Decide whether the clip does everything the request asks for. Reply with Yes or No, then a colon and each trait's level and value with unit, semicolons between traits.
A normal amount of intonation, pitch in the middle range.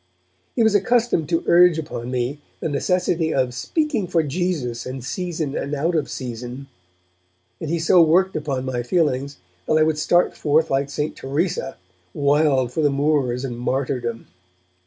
Yes: average, 4.5 semitones; medium, 150 Hz